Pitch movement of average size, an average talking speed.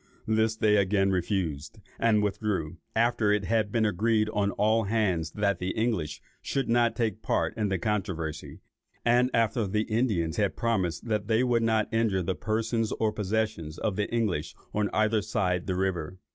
Yes: average, 3.0 semitones; average, 175 wpm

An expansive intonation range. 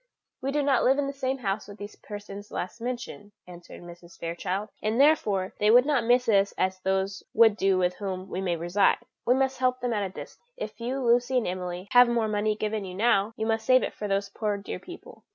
No: average, 4.3 semitones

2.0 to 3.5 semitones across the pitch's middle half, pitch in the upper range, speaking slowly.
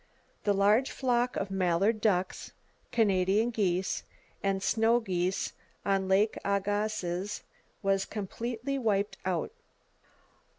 Yes: narrow, 2.6 semitones; high, 200 Hz; slow, 100 wpm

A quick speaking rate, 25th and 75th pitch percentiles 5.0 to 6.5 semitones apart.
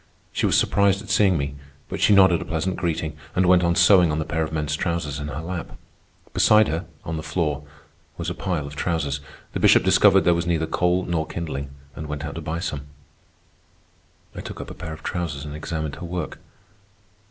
No: fast, 210 wpm; average, 2.8 semitones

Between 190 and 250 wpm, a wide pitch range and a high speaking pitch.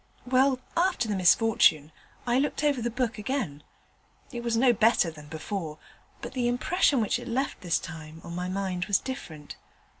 No: average, 175 wpm; wide, 6.5 semitones; high, 225 Hz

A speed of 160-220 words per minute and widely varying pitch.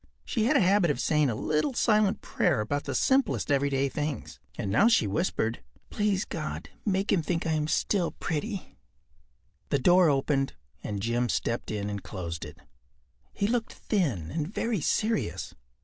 Yes: average, 165 wpm; wide, 8.8 semitones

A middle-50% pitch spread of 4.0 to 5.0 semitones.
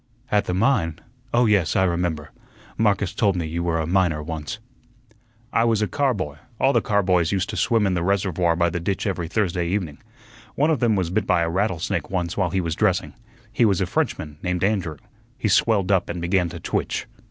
No: average, 3.2 semitones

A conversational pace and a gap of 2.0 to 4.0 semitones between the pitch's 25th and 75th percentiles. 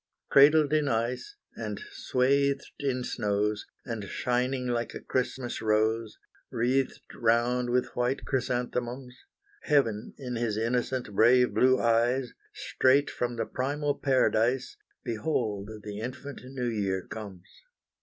No: slow, 120 wpm; average, 2.8 semitones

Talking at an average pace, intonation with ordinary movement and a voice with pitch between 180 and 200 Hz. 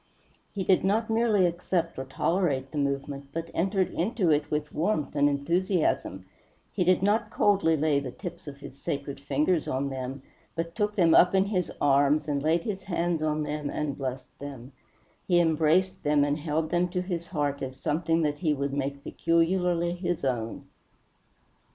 No: average, 175 wpm; average, 4.0 semitones; medium, 160 Hz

